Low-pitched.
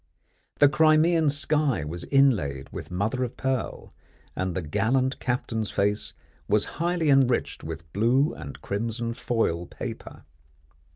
Yes: low, 115 Hz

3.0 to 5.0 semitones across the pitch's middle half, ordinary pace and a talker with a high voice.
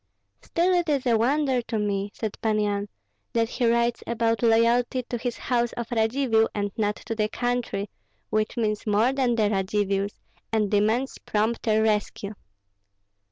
No: narrow, 2.4 semitones; average, 160 wpm; high, 225 Hz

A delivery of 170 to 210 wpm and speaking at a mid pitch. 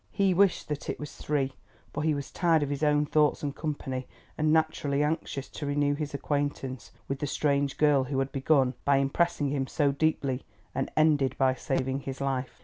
Yes: average, 195 wpm; medium, 145 Hz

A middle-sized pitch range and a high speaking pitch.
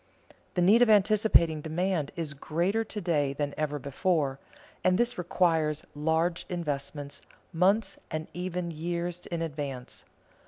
No: average, 3.5 semitones; medium, 165 Hz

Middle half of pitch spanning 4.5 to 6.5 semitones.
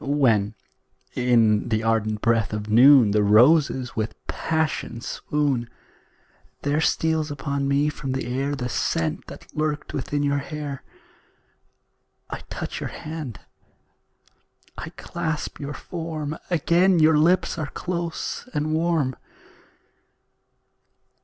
Yes: average, 4.8 semitones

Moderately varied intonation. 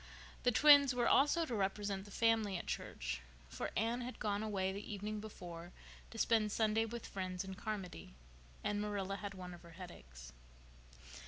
Yes: average, 3.3 semitones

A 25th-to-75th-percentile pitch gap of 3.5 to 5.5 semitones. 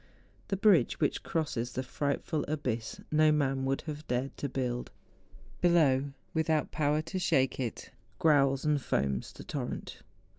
No: average, 3.1 semitones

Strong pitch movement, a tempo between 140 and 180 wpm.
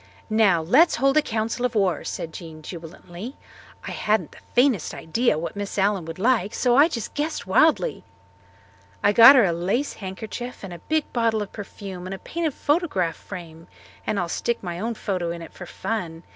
No: wide, 5.7 semitones; average, 190 wpm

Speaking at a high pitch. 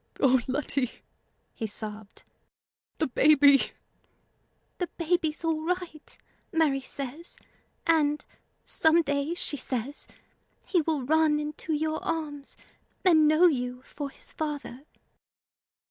Yes: very high, 300 Hz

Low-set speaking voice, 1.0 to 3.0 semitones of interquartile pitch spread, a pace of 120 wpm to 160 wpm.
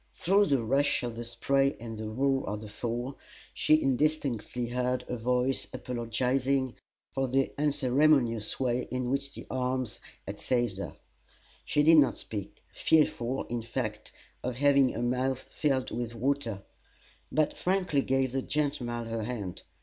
Yes: low, 125 Hz; average, 2.7 semitones; average, 150 wpm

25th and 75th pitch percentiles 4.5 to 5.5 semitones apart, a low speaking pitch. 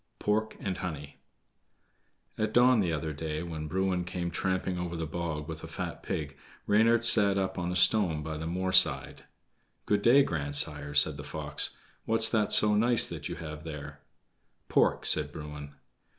Yes: average, 5.1 semitones; very low, 85 Hz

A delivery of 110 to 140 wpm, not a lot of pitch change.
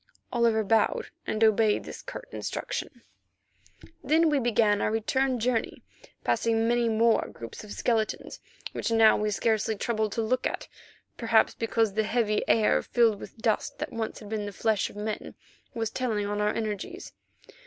No: average, 165 wpm; narrow, 1.5 semitones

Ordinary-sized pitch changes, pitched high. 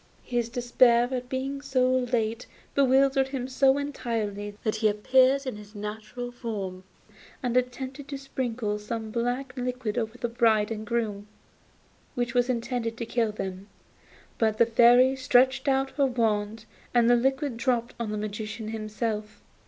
Yes: average, 3.0 semitones; high, 240 Hz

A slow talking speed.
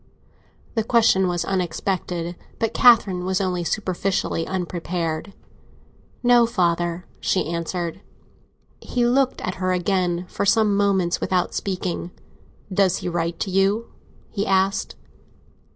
Yes: slow, 120 wpm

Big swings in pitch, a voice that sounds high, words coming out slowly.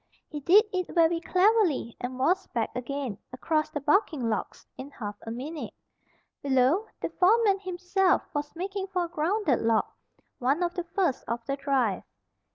No: wide, 6.1 semitones; very high, 310 Hz; average, 165 wpm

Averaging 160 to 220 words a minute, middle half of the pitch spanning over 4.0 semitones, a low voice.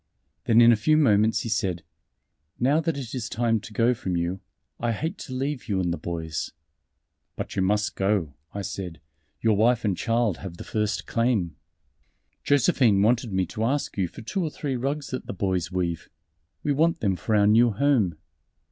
Yes: average, 190 wpm; average, 4.8 semitones; low, 110 Hz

